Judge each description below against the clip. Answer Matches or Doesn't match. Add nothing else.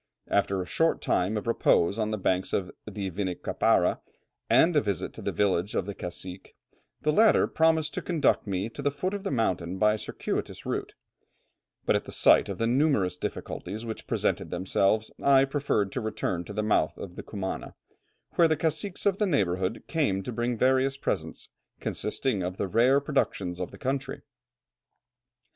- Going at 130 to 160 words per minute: Doesn't match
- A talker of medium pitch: Doesn't match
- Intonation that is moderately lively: Doesn't match